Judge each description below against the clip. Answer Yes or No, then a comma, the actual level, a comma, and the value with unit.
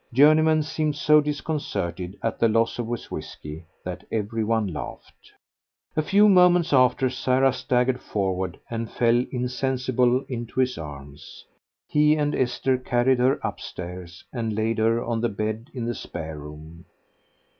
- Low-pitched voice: Yes, low, 120 Hz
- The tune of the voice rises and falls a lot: No, average, 4.5 semitones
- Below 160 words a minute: Yes, average, 145 wpm